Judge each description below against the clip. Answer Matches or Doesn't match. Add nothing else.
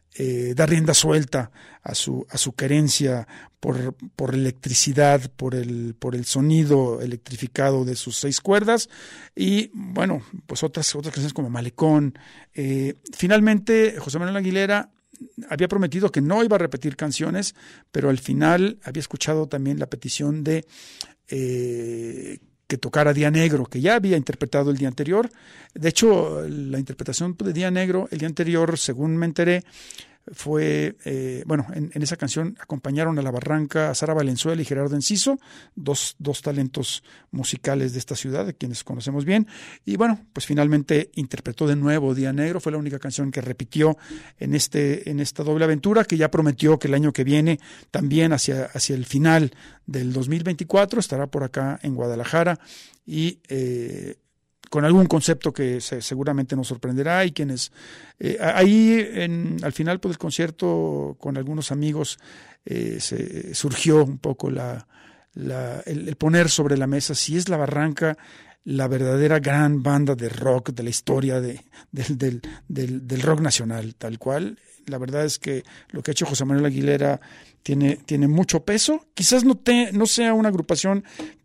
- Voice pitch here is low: Doesn't match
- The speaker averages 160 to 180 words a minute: Matches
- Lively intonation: Doesn't match